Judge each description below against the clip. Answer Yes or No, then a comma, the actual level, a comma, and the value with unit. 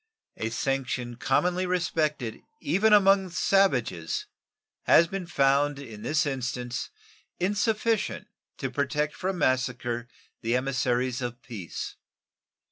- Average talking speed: No, slow, 105 wpm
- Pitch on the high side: No, low, 135 Hz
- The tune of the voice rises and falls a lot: Yes, wide, 6.6 semitones